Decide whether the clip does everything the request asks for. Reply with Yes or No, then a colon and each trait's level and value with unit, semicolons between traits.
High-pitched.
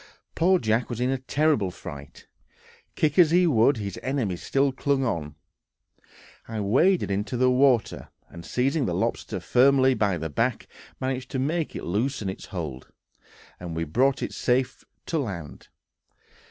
No: low, 125 Hz